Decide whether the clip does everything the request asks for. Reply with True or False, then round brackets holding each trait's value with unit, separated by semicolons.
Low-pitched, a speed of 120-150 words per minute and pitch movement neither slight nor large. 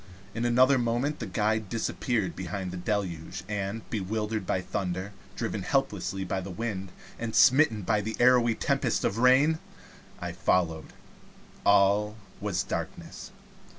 True (105 Hz; 140 wpm; 3.7 semitones)